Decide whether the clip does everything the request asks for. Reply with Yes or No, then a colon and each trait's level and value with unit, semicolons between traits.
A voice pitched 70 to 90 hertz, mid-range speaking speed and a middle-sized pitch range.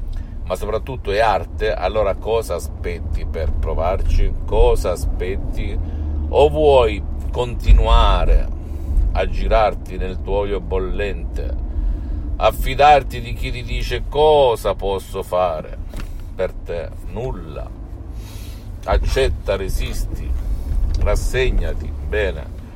No: very low, 85 Hz; slow, 90 wpm; average, 4.2 semitones